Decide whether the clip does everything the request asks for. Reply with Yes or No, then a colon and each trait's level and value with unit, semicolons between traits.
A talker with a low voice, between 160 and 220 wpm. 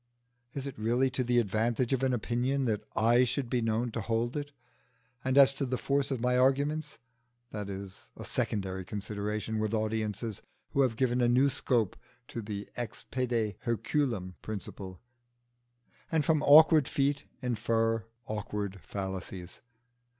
No: low, 120 Hz; average, 150 wpm